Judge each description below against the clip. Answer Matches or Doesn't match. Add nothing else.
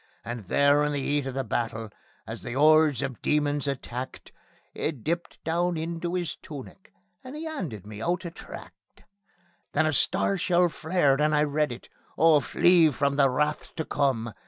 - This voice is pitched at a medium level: Matches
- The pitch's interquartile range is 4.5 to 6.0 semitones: Doesn't match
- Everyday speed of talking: Matches